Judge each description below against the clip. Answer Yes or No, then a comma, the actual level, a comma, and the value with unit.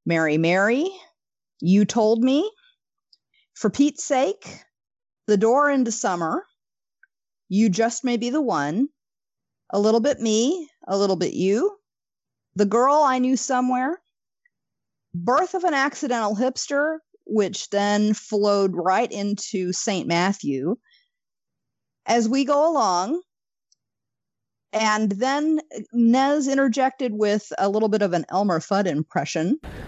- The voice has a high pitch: Yes, high, 235 Hz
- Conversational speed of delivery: No, slow, 120 wpm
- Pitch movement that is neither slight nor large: No, wide, 5.9 semitones